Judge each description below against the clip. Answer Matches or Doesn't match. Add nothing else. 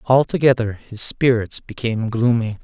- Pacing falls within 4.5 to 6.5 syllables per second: Matches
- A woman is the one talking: Doesn't match